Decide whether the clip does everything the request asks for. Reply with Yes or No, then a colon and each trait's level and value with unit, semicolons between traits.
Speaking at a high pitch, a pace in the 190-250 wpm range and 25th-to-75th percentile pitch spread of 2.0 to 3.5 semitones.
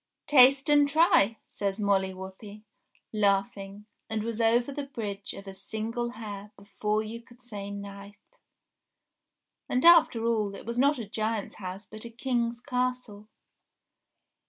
No: high, 220 Hz; average, 140 wpm; average, 3.2 semitones